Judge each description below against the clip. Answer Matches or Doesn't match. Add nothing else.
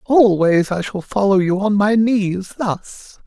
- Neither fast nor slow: Matches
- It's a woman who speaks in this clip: Doesn't match